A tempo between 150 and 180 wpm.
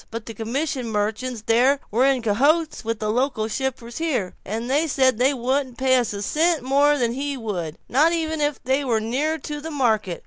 No: average, 200 wpm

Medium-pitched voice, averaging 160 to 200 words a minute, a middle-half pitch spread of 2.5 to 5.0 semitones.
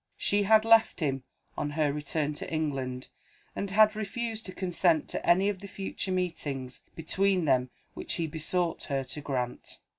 No: medium, 165 Hz; average, 170 wpm; wide, 5.5 semitones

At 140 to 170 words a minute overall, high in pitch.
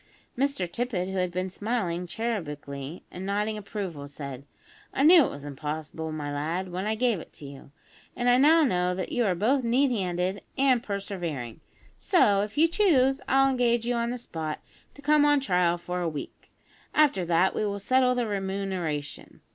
No: average, 185 wpm; high, 195 Hz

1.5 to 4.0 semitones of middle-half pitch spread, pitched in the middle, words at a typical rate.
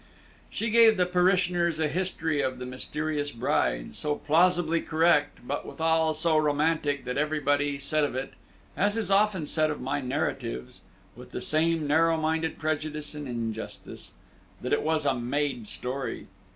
Yes: narrow, 2.5 semitones; medium, 155 Hz; average, 155 wpm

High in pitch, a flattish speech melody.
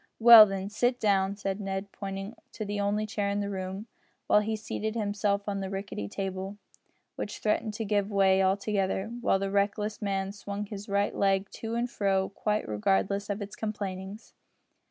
Yes: high, 200 Hz; narrow, 1.4 semitones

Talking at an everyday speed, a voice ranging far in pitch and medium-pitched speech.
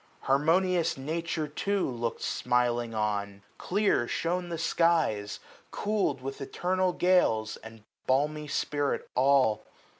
No: slow, 110 wpm; wide, 6.3 semitones; medium, 145 Hz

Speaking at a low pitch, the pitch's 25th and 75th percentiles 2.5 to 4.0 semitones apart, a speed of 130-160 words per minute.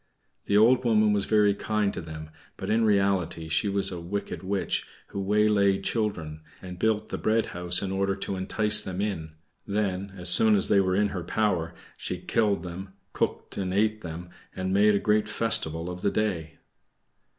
No: low, 100 Hz; average, 2.9 semitones; average, 185 wpm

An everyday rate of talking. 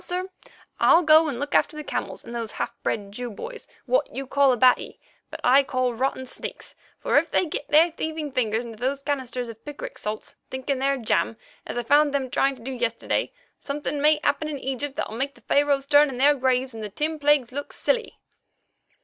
No: fast, 215 wpm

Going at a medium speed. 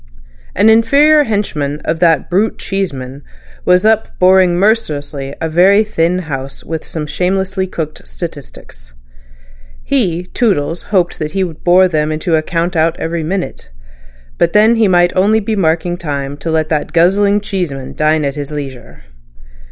Yes: average, 150 wpm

